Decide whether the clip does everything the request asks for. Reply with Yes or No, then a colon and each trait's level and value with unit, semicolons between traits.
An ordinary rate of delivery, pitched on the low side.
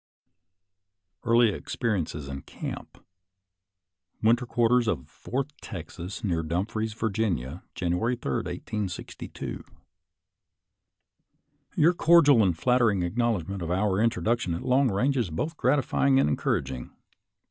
No: slow, 110 wpm; low, 110 Hz